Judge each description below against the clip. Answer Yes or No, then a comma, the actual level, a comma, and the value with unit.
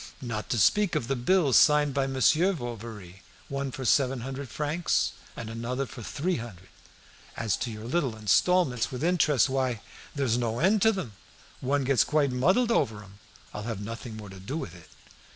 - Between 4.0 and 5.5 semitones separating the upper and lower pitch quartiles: Yes, average, 4.5 semitones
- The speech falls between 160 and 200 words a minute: Yes, average, 190 wpm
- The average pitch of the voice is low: Yes, low, 130 Hz